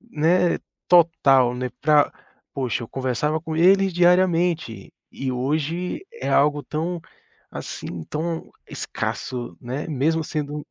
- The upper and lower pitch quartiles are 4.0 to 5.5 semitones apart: Yes, average, 4.5 semitones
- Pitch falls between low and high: Yes, medium, 155 Hz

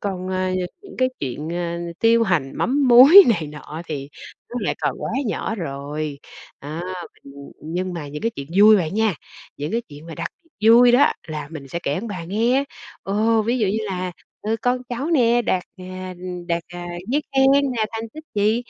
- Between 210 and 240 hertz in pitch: No, high, 190 Hz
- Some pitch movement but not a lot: No, wide, 6.1 semitones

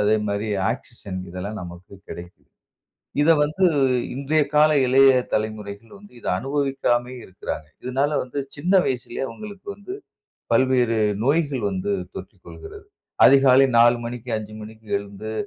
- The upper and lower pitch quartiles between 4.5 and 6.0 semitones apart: Yes, average, 5.0 semitones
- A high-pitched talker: No, low, 125 Hz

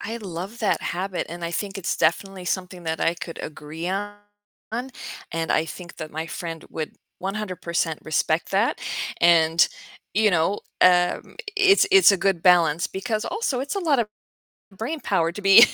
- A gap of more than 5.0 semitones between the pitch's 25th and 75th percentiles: No, average, 4.2 semitones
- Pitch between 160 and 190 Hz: Yes, medium, 185 Hz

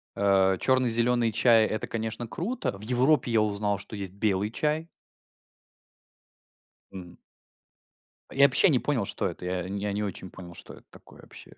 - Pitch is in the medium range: No, low, 110 Hz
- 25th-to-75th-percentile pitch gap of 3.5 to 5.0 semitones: Yes, average, 4.0 semitones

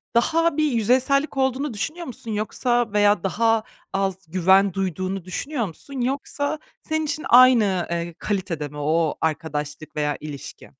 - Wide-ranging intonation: Yes, wide, 7.4 semitones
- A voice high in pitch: Yes, high, 205 Hz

